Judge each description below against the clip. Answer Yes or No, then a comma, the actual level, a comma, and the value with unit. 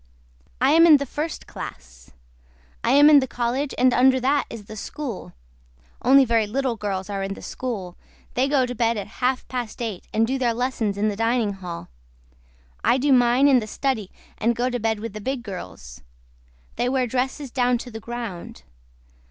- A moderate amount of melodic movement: Yes, average, 3.6 semitones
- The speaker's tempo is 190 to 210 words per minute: Yes, average, 195 wpm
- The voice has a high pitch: Yes, high, 240 Hz